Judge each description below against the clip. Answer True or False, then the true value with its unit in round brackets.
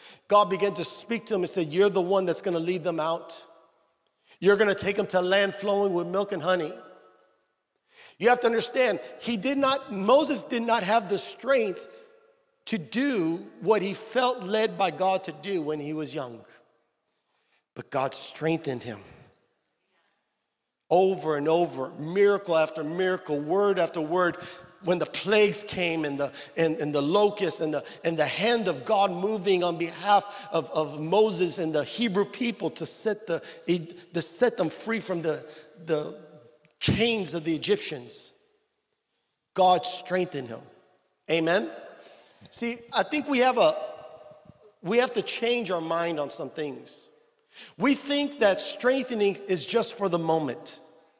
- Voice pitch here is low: False (185 Hz)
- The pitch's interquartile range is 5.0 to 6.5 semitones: True (5.6 semitones)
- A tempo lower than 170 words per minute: True (160 wpm)